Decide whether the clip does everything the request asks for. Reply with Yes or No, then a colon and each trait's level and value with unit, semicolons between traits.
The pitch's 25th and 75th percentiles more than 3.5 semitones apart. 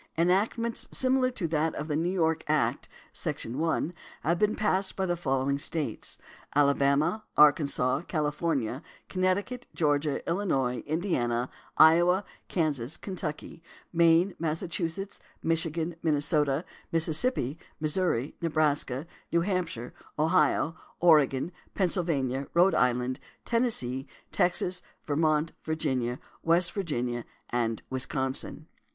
Yes: average, 4.1 semitones